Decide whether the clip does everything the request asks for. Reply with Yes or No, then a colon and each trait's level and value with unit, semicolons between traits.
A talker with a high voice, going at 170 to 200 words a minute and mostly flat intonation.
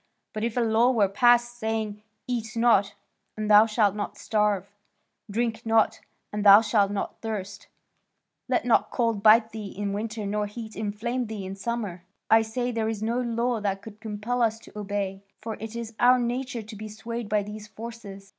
Yes: high, 220 Hz; average, 185 wpm; narrow, 2.0 semitones